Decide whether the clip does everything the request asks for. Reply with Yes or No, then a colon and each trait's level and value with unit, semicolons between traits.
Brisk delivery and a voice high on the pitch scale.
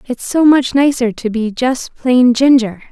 No: average, 185 wpm; very high, 250 Hz